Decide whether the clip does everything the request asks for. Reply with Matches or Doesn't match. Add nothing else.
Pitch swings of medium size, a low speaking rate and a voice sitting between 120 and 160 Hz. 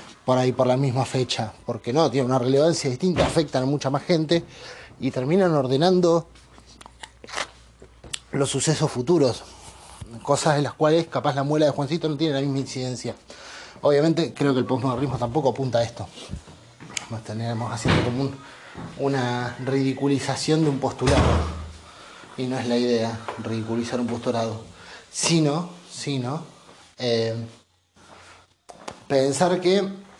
Doesn't match